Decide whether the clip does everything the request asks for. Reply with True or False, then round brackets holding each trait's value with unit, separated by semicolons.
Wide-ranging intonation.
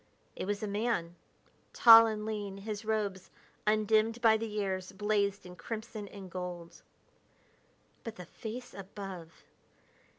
False (2.5 semitones)